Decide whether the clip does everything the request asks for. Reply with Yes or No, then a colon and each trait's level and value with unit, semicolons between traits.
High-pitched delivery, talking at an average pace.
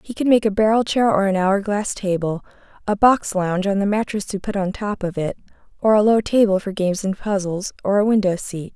No: high, 200 Hz; fast, 240 wpm